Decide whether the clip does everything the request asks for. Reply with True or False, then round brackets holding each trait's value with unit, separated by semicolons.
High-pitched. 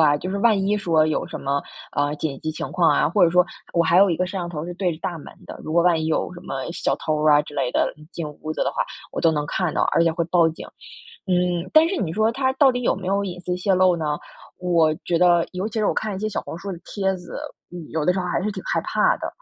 False (175 Hz)